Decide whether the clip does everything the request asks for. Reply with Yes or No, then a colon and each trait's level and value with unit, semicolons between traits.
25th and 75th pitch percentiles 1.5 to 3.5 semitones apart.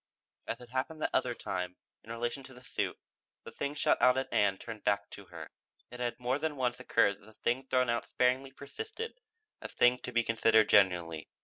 Yes: average, 3.2 semitones